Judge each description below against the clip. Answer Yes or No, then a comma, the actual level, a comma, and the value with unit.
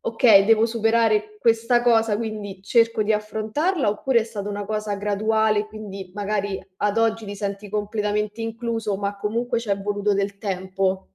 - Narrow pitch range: Yes, narrow, 1.8 semitones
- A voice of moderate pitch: No, high, 210 Hz